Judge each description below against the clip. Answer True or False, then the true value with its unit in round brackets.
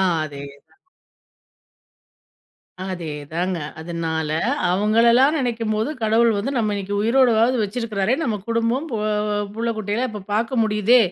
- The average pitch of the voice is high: True (220 Hz)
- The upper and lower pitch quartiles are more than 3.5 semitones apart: False (3.2 semitones)